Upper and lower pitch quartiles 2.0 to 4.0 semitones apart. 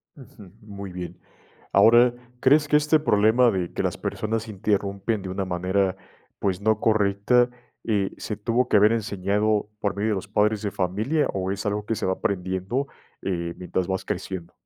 Yes: average, 2.8 semitones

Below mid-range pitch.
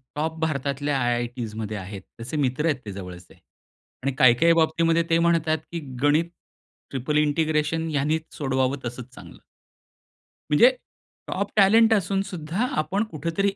No: medium, 150 Hz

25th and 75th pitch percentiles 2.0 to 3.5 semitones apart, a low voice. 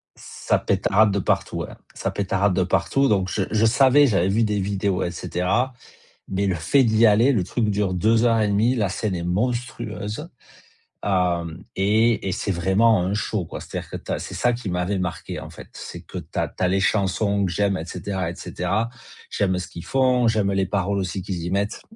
Yes: average, 3.1 semitones; low, 100 Hz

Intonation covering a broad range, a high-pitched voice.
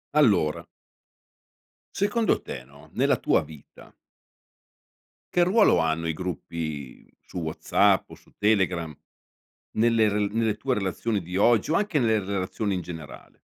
No: wide, 6.0 semitones; very low, 95 Hz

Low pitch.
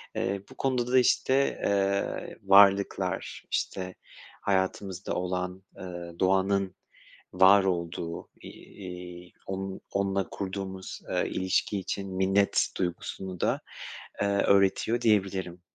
Yes: very low, 95 Hz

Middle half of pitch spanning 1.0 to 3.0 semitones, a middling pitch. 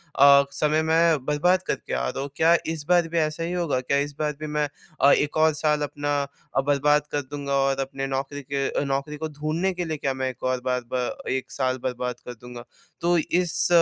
Yes: average, 2.7 semitones; medium, 145 Hz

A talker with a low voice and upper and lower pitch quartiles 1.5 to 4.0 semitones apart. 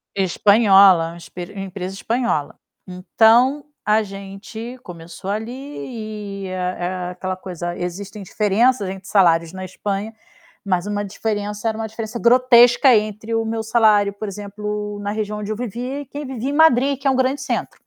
No: high, 210 Hz; average, 3.4 semitones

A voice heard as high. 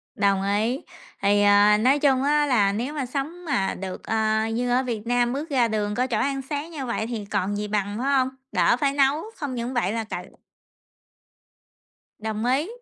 Yes: high, 240 Hz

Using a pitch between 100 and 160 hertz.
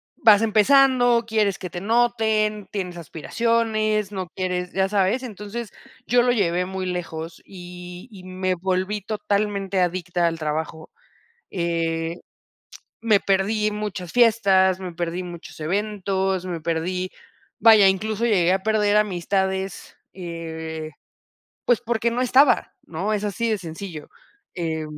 No: high, 190 Hz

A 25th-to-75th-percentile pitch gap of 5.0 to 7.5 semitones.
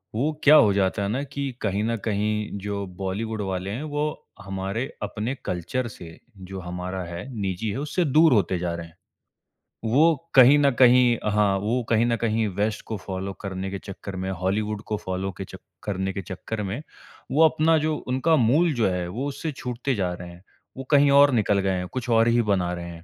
Yes: average, 5.3 semitones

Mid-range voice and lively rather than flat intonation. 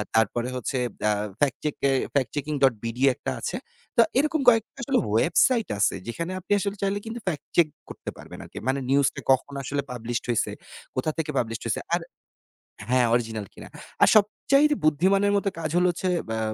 Yes: medium, 145 Hz; wide, 8.4 semitones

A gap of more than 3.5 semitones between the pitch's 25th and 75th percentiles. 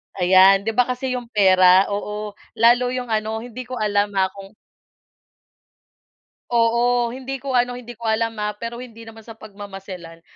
No: average, 3.2 semitones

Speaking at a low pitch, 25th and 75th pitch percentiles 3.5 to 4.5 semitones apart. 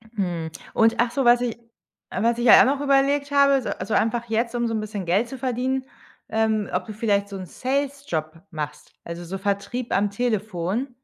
No: high, 225 Hz; average, 4.2 semitones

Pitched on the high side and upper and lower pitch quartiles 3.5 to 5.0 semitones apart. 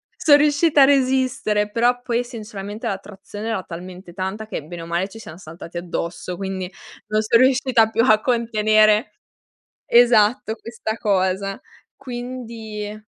Yes: high, 215 Hz; average, 3.9 semitones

